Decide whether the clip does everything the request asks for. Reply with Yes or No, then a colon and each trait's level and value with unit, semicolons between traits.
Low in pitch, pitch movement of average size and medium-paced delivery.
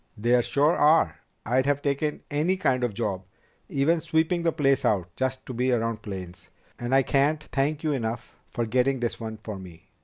Yes: low, 130 Hz; average, 4.6 semitones; average, 190 wpm